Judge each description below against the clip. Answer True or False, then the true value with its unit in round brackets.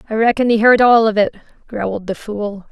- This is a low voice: False (220 Hz)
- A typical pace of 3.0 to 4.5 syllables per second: False (5.6 syllables/s)